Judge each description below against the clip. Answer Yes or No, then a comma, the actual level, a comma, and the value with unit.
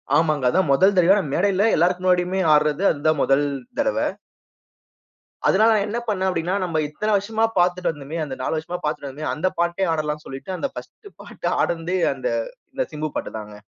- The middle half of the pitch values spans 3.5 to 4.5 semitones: Yes, average, 4.1 semitones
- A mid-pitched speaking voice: Yes, medium, 175 Hz